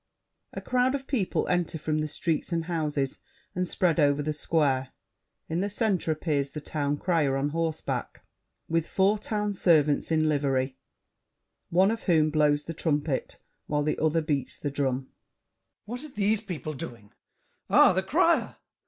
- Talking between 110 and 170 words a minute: Yes, average, 160 wpm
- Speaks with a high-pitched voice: No, medium, 155 Hz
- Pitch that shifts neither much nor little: Yes, average, 3.7 semitones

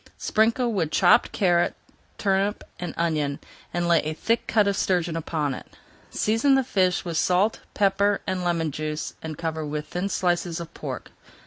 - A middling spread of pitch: Yes, average, 3.8 semitones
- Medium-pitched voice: Yes, medium, 175 Hz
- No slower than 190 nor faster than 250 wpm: No, average, 165 wpm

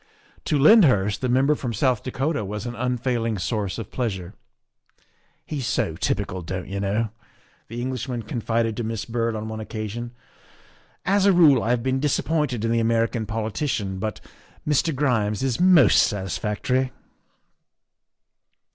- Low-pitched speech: Yes, low, 115 Hz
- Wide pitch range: No, average, 3.5 semitones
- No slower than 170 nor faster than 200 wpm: No, average, 150 wpm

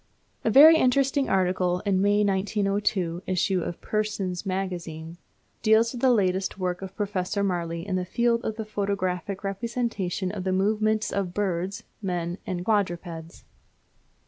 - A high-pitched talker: Yes, high, 195 Hz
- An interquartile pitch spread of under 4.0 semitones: Yes, average, 2.8 semitones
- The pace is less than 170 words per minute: Yes, average, 145 wpm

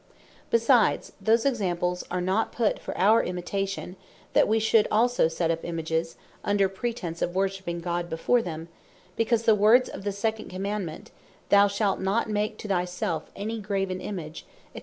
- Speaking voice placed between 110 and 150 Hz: No, high, 195 Hz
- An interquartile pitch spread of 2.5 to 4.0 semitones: Yes, average, 3.6 semitones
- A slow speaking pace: No, average, 165 wpm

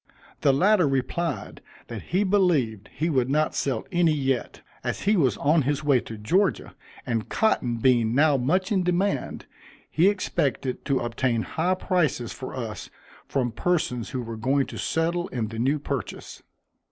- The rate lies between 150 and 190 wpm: Yes, average, 165 wpm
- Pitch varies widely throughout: Yes, wide, 6.2 semitones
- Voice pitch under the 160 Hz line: Yes, medium, 140 Hz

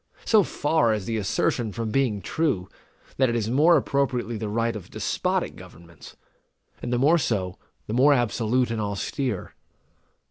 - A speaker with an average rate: Yes, average, 155 wpm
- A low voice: Yes, low, 115 Hz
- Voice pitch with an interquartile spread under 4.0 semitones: No, average, 4.3 semitones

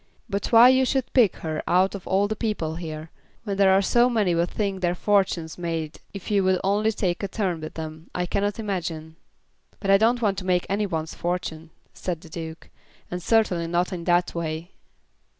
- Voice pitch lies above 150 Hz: Yes, medium, 185 Hz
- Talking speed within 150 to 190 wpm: No, fast, 205 wpm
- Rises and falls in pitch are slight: No, average, 3.5 semitones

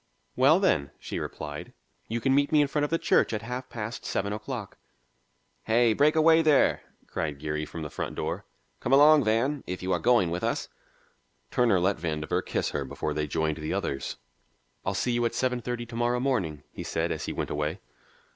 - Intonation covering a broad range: Yes, wide, 8.4 semitones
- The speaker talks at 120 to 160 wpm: No, fast, 205 wpm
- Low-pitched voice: Yes, low, 115 Hz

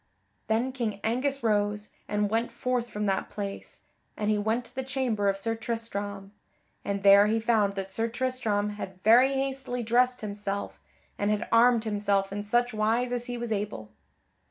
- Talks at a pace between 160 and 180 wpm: Yes, average, 175 wpm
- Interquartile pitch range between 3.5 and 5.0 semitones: No, average, 2.9 semitones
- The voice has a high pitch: Yes, high, 220 Hz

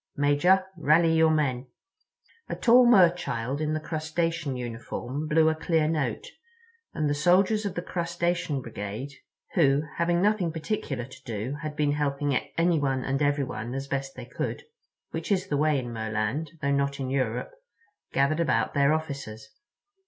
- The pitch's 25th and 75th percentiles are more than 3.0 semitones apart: Yes, average, 3.5 semitones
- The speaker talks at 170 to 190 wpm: No, average, 155 wpm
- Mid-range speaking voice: Yes, medium, 150 Hz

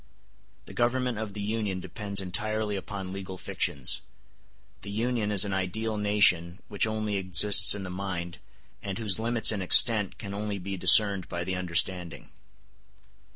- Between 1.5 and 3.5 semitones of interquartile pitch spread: Yes, narrow, 2.5 semitones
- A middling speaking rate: Yes, average, 155 wpm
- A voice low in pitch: Yes, low, 100 Hz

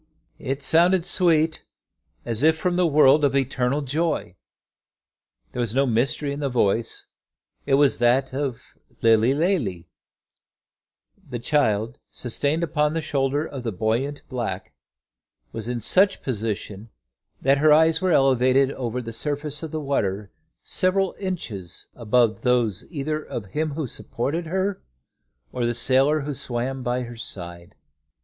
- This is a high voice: No, low, 135 Hz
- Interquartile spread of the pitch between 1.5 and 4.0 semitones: No, average, 4.5 semitones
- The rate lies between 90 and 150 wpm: Yes, average, 145 wpm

